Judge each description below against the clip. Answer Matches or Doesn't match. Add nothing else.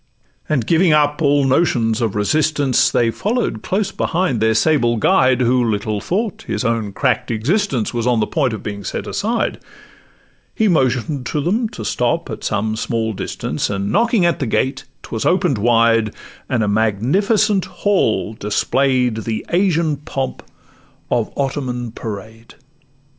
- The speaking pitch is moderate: Doesn't match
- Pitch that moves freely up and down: Matches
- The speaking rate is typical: Matches